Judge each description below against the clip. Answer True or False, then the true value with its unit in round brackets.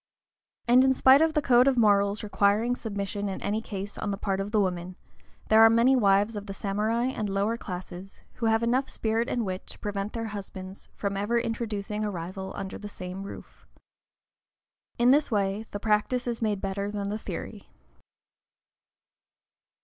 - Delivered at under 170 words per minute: False (180 wpm)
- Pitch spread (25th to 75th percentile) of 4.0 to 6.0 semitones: False (2.7 semitones)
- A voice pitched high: True (210 Hz)